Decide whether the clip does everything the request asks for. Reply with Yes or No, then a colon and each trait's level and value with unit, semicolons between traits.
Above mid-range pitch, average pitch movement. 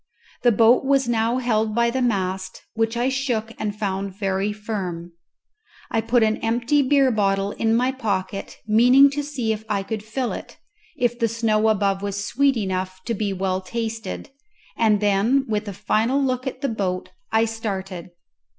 Yes: high, 220 Hz; average, 3.4 semitones